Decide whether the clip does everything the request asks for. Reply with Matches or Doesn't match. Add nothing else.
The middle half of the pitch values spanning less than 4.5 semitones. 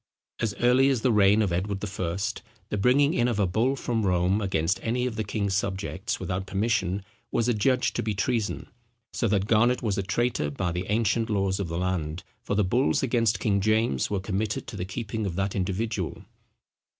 Matches